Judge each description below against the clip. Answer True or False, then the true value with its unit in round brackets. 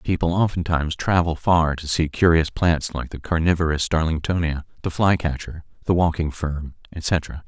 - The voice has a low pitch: True (80 Hz)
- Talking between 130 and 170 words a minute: True (150 wpm)